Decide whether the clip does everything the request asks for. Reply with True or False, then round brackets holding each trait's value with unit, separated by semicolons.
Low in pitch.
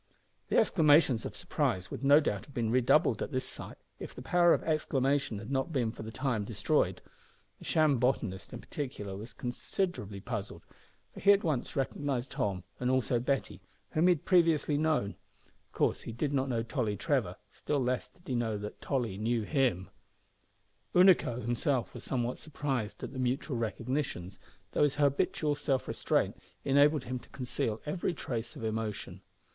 True (130 Hz)